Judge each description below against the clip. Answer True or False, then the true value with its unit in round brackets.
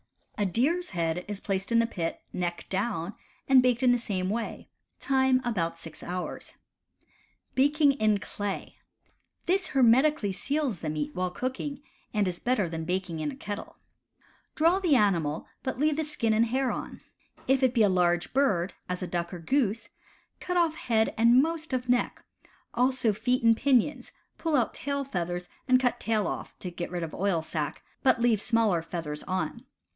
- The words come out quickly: False (180 wpm)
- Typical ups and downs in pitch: False (6.6 semitones)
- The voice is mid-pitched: False (225 Hz)